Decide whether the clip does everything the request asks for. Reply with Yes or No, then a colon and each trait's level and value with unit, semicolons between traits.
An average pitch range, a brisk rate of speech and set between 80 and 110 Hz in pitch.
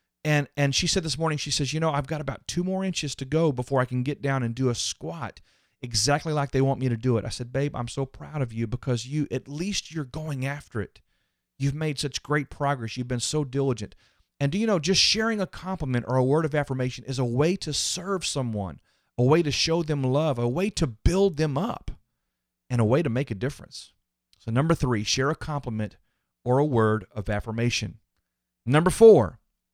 No: average, 4.4 semitones; fast, 225 wpm; low, 135 Hz